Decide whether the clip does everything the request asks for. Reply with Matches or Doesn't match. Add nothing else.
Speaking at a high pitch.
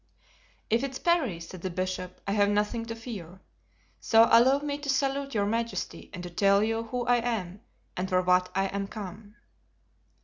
Matches